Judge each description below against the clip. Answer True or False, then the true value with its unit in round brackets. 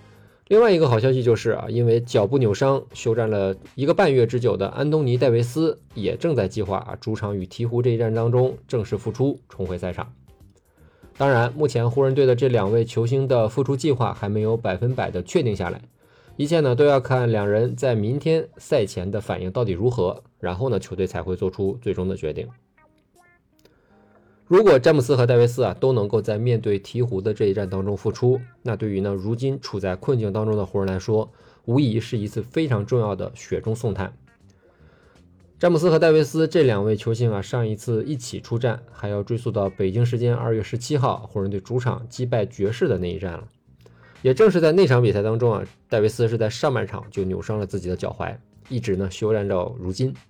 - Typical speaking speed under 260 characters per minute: False (310 characters per minute)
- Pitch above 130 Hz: False (115 Hz)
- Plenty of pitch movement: False (4.2 semitones)